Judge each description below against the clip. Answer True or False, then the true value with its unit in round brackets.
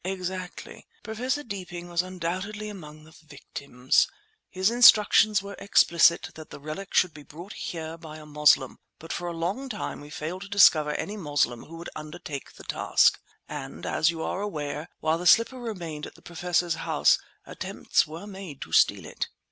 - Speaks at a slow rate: False (175 wpm)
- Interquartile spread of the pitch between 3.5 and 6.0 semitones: True (4.3 semitones)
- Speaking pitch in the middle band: True (175 Hz)